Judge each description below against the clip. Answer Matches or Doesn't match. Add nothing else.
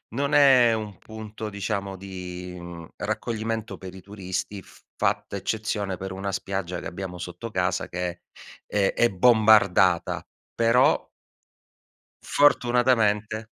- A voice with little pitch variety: Doesn't match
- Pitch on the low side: Matches